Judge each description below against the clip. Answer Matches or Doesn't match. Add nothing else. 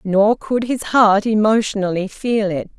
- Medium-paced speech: Matches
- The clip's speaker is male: Doesn't match